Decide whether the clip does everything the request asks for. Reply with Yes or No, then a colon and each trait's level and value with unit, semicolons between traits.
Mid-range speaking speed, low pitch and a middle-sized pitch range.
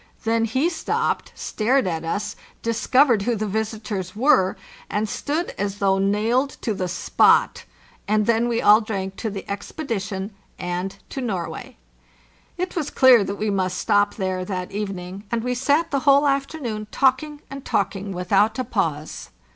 No: average, 170 wpm; high, 215 Hz; average, 4.8 semitones